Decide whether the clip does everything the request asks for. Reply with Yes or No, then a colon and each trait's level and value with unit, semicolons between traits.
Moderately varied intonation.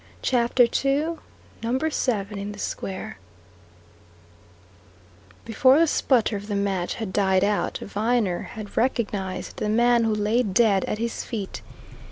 Yes: average, 3.3 semitones